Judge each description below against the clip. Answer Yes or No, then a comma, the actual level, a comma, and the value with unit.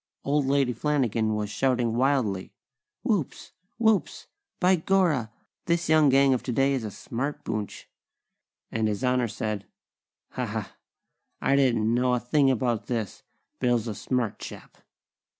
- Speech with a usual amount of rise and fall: Yes, average, 3.8 semitones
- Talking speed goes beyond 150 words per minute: No, average, 140 wpm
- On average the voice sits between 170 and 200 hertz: No, low, 125 Hz